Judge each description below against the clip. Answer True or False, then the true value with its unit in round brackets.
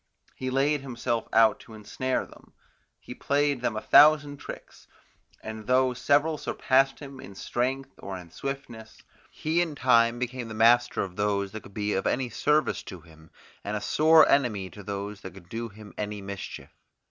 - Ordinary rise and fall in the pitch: True (4.7 semitones)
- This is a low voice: True (115 Hz)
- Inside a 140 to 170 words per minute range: False (180 wpm)